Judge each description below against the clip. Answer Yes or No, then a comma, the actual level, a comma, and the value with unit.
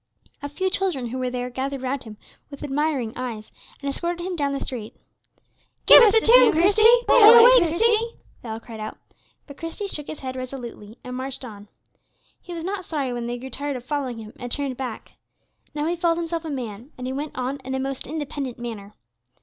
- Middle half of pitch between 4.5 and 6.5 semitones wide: Yes, average, 5.1 semitones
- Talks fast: Yes, fast, 210 wpm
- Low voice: No, very high, 275 Hz